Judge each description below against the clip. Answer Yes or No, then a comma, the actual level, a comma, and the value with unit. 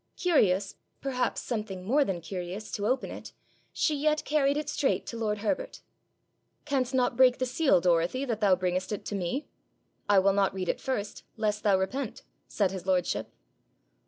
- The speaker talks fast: No, average, 175 wpm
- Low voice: No, high, 215 Hz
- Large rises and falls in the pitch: Yes, wide, 5.9 semitones